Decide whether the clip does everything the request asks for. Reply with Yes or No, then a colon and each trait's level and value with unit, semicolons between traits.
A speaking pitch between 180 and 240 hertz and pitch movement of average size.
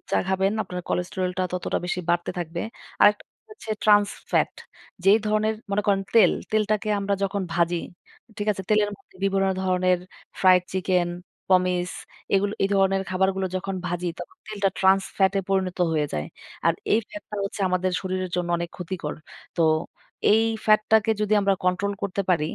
No: high, 190 Hz; narrow, 2.0 semitones